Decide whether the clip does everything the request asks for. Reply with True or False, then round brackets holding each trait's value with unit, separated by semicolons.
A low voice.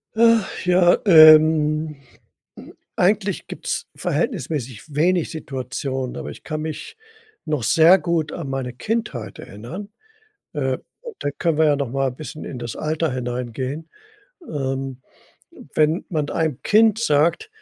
False (155 Hz)